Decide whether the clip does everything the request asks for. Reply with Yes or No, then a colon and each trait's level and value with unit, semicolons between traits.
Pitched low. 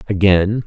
Yes: low, 100 Hz